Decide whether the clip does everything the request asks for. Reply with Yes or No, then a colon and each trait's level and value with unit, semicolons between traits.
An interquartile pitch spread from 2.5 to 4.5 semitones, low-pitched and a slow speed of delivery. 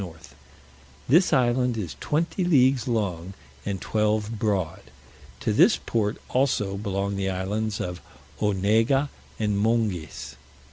Yes: average, 4.0 semitones; low, 105 Hz; slow, 120 wpm